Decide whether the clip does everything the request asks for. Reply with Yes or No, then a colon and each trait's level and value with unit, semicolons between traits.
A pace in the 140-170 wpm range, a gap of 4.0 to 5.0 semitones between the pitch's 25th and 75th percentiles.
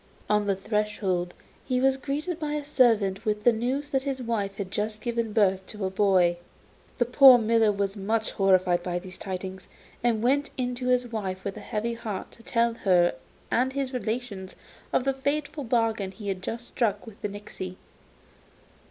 No: average, 185 wpm; average, 4.3 semitones